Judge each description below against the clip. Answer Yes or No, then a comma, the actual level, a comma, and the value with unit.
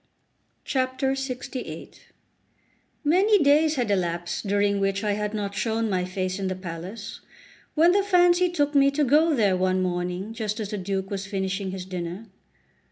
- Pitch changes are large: Yes, wide, 6.7 semitones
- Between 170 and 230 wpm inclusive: No, average, 160 wpm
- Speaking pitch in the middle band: No, high, 205 Hz